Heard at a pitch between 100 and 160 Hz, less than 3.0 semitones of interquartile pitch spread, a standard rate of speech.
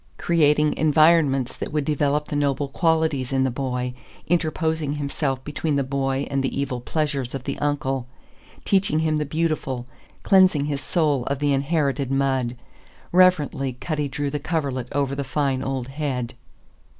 Yes: medium, 140 Hz; narrow, 2.4 semitones; average, 155 wpm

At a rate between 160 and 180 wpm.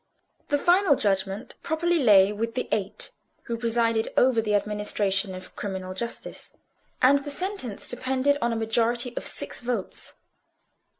No: average, 140 wpm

